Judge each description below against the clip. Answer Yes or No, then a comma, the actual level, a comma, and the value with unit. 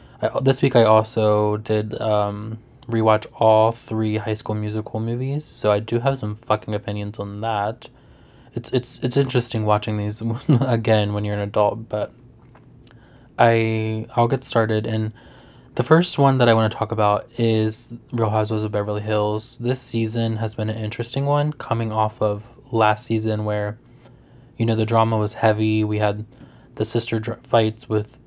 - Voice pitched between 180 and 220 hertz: No, low, 110 Hz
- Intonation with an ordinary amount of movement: No, narrow, 1.7 semitones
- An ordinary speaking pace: Yes, average, 170 wpm